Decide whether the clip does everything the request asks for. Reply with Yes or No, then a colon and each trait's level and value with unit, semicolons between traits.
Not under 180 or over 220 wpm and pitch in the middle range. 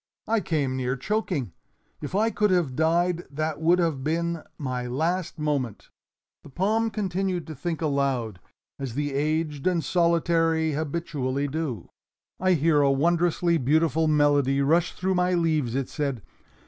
No: average, 145 wpm; medium, 160 Hz